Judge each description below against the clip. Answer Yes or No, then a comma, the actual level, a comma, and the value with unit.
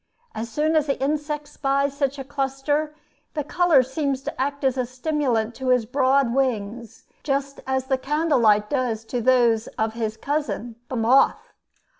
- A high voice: Yes, very high, 265 Hz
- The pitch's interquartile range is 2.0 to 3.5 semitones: Yes, average, 3.2 semitones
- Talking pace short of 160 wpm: No, average, 170 wpm